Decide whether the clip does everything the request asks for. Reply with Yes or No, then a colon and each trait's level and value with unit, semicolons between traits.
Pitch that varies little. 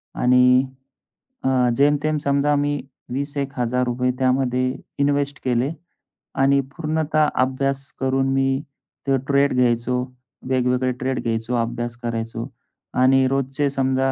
Yes: narrow, 1.8 semitones